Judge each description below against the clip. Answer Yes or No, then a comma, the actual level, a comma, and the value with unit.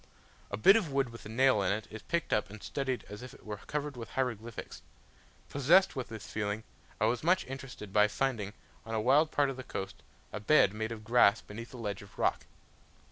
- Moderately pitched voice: No, low, 115 Hz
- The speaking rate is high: Yes, fast, 220 wpm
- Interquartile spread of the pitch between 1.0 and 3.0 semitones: No, average, 4.2 semitones